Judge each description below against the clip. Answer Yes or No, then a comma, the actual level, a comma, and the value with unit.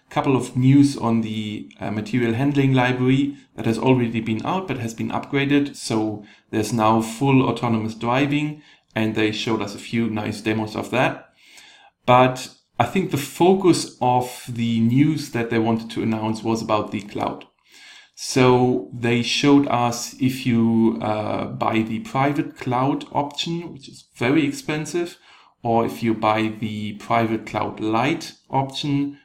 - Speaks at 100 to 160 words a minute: Yes, average, 155 wpm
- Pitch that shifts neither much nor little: Yes, average, 3.8 semitones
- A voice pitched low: Yes, low, 120 Hz